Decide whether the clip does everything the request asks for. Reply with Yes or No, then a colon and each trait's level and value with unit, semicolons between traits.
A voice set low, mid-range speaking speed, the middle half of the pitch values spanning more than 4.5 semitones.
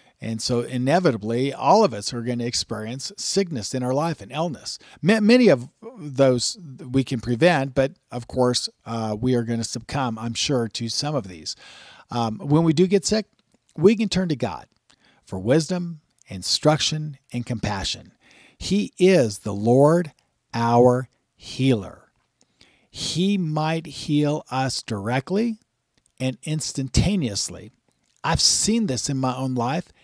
Yes: low, 130 Hz; average, 145 wpm; wide, 5.4 semitones